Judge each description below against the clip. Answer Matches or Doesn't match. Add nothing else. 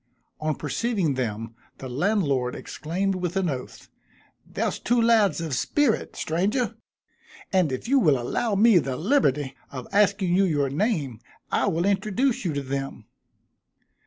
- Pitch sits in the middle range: Matches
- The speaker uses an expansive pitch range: Matches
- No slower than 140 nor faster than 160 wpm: Matches